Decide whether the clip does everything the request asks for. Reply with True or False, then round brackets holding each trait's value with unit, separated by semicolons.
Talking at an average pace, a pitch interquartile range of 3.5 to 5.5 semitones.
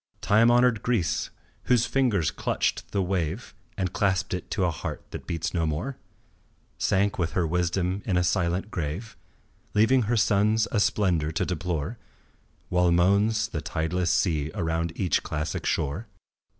True (150 wpm; 4.1 semitones)